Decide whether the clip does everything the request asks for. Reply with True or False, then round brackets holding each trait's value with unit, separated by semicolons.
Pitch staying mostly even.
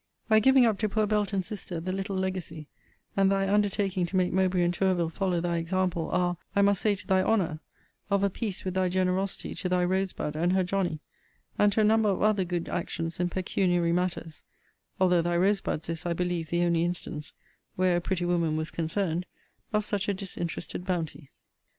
True (2.2 semitones)